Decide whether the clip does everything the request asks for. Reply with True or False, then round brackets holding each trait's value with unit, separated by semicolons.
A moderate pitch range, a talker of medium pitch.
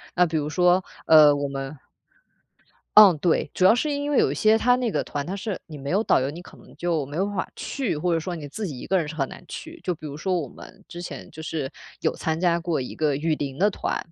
True (4.5 semitones; 170 Hz)